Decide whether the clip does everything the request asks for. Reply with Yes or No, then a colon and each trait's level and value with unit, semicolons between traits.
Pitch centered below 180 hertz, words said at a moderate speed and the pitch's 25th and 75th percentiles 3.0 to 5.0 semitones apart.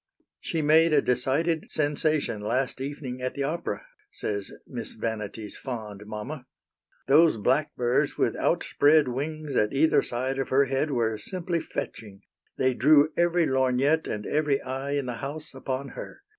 Yes: low, 135 Hz; average, 150 wpm; average, 3.9 semitones